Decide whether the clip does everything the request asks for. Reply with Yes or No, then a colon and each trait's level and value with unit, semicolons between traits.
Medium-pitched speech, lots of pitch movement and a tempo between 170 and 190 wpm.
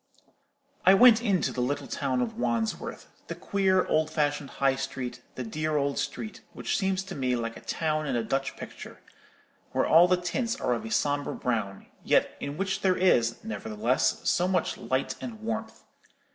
Yes: medium, 145 Hz; wide, 7.2 semitones; average, 180 wpm